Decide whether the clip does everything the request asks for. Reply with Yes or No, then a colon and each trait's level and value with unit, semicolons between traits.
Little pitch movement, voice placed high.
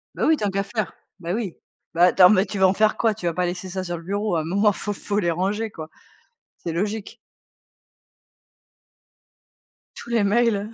No: average, 3.1 semitones; high, 200 Hz